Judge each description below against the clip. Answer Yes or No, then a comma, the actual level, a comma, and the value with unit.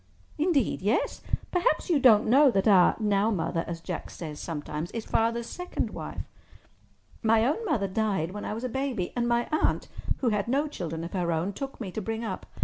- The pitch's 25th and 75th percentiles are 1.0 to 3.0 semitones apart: No, wide, 5.6 semitones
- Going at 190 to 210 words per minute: Yes, average, 200 wpm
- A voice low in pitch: No, high, 220 Hz